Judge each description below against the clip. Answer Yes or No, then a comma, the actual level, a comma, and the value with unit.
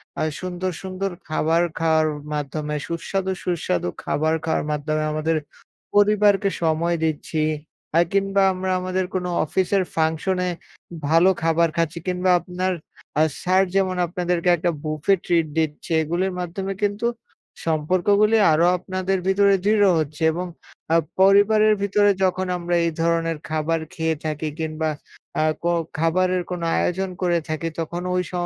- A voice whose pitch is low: No, medium, 175 Hz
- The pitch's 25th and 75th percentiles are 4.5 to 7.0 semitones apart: No, average, 2.9 semitones